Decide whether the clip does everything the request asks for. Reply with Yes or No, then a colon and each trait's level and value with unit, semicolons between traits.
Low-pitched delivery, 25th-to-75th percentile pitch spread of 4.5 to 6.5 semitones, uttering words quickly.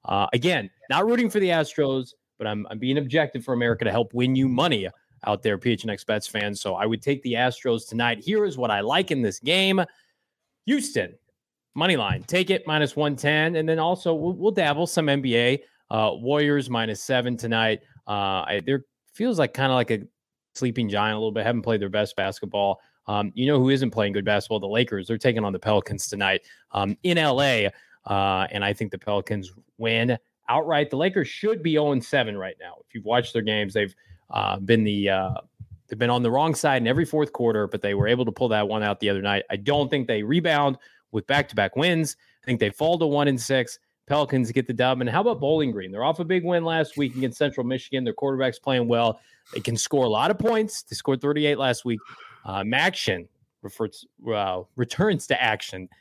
Yes: low, 125 Hz; average, 5.3 semitones; fast, 215 wpm